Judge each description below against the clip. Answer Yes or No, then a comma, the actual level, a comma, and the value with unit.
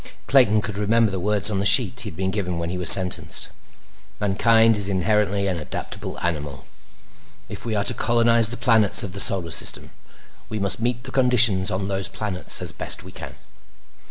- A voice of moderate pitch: No, low, 100 Hz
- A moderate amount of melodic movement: Yes, average, 3.2 semitones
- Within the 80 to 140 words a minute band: No, average, 190 wpm